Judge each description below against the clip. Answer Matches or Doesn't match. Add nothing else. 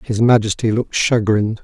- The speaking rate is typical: Matches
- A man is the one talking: Matches